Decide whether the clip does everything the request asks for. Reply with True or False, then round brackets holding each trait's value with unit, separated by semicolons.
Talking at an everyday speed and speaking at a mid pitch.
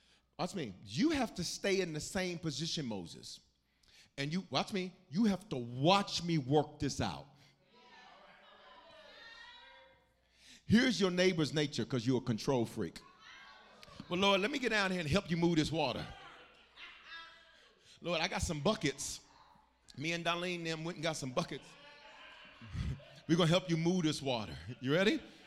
True (165 wpm; 170 Hz)